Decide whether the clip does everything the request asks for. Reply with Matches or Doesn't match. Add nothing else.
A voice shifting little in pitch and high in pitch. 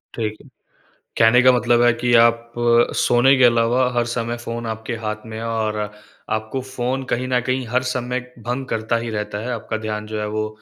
Doesn't match